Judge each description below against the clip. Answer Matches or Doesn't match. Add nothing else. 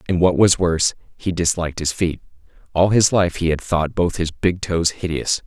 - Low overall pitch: Matches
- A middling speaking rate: Doesn't match